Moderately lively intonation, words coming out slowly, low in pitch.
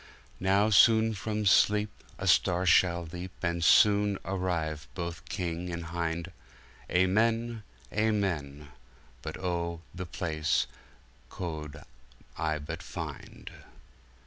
Yes: average, 3.4 semitones; slow, 90 wpm; very low, 90 Hz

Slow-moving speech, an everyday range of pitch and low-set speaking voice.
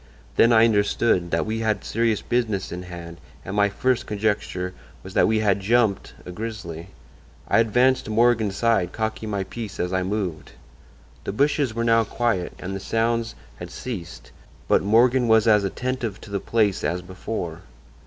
No: average, 175 wpm; average, 3.5 semitones; low, 110 Hz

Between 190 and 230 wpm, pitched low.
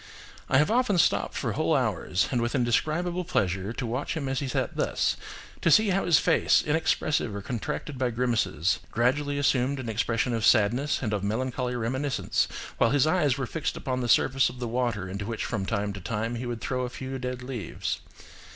Yes: average, 195 wpm; low, 125 Hz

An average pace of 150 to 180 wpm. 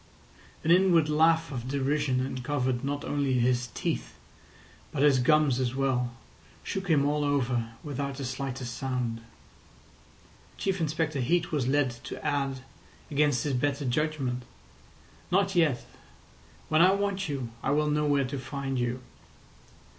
No: average, 140 wpm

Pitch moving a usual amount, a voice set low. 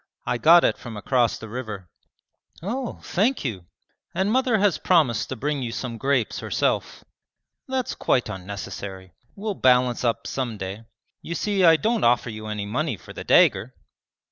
No: wide, 8.9 semitones; low, 125 Hz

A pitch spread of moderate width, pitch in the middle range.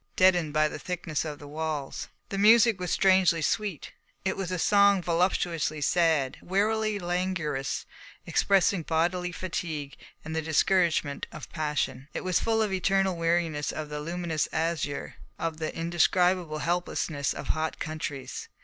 Yes: average, 3.3 semitones; medium, 170 Hz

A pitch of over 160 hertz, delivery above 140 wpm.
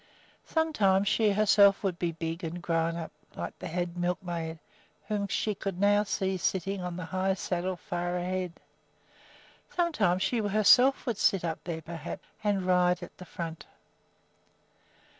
Yes: medium, 185 Hz; average, 150 wpm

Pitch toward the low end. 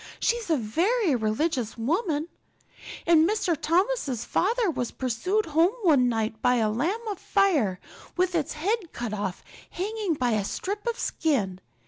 No: very high, 315 Hz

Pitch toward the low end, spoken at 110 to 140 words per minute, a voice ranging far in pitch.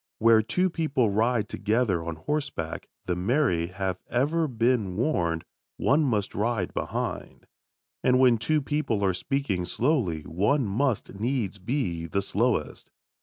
Yes: low, 110 Hz; slow, 135 wpm; wide, 6.5 semitones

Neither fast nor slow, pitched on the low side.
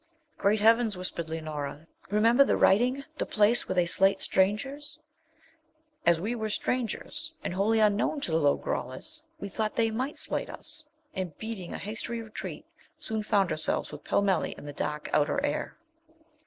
No: average, 165 wpm; high, 210 Hz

